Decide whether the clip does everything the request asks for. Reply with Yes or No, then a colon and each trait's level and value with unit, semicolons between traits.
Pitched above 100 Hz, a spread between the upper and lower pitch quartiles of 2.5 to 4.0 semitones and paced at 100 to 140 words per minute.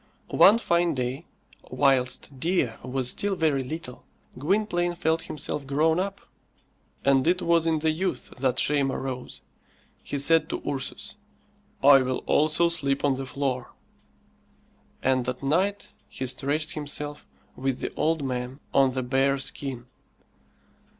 Yes: medium, 140 Hz; average, 3.7 semitones; slow, 135 wpm